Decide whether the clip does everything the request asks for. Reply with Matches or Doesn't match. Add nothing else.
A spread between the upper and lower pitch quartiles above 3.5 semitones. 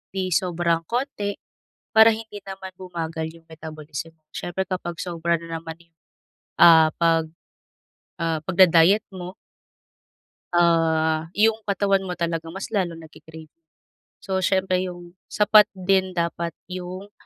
Doesn't match